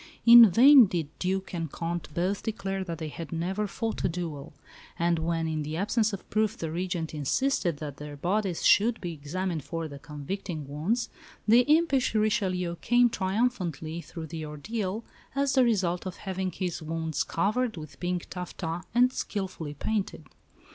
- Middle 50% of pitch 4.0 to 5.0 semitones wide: Yes, average, 4.7 semitones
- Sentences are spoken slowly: No, average, 165 wpm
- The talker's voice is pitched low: No, medium, 180 Hz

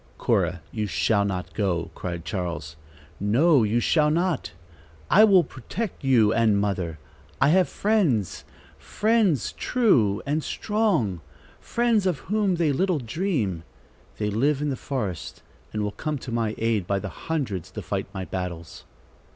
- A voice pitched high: No, low, 120 Hz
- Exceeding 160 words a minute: No, average, 150 wpm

